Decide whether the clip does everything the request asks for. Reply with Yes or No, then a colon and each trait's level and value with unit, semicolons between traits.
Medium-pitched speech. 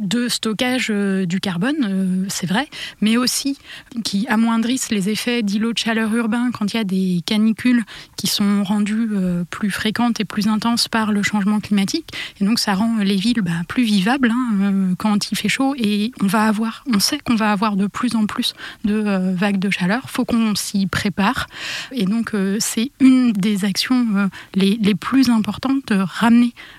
No: high, 215 Hz